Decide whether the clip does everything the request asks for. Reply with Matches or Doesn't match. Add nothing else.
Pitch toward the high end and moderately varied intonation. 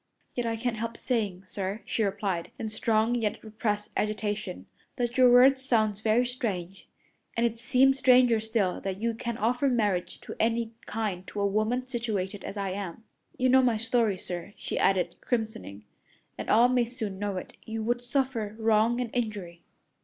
Matches